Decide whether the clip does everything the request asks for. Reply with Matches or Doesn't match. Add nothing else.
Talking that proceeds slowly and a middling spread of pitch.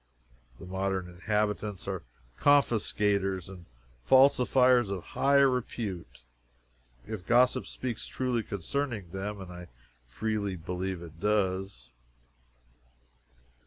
Matches